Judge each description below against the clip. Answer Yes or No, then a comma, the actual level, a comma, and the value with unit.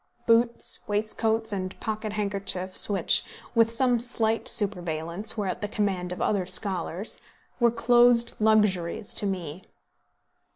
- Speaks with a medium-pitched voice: No, high, 210 Hz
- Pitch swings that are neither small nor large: Yes, average, 3.4 semitones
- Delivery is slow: Yes, slow, 125 wpm